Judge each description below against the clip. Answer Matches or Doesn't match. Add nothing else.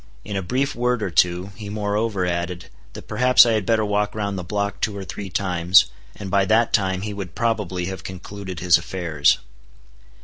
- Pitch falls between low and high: Doesn't match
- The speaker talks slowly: Doesn't match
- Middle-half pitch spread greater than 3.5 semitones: Doesn't match